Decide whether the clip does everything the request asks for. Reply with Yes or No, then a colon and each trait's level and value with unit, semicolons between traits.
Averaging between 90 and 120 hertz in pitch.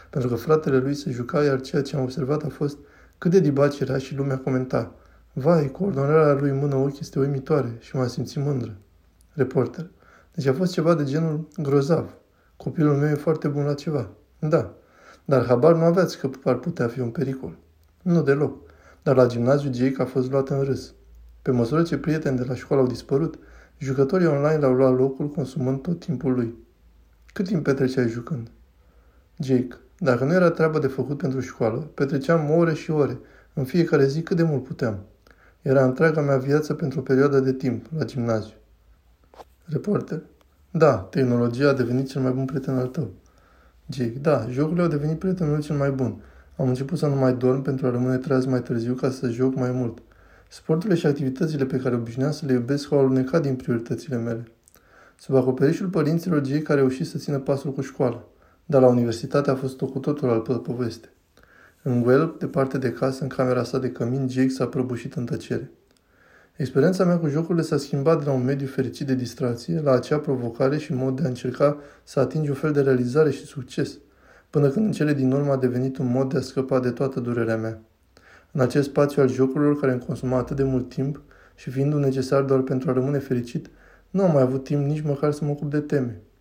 No: low, 135 Hz